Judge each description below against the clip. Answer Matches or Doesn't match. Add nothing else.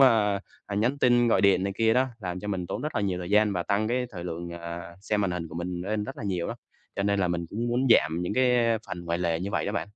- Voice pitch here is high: Doesn't match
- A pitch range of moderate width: Matches